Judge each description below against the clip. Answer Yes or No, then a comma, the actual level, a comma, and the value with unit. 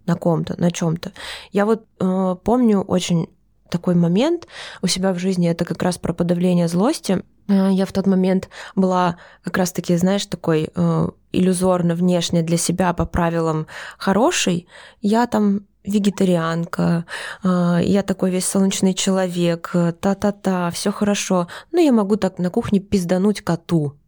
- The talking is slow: No, average, 150 wpm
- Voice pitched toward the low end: No, medium, 185 Hz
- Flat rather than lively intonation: Yes, narrow, 2.3 semitones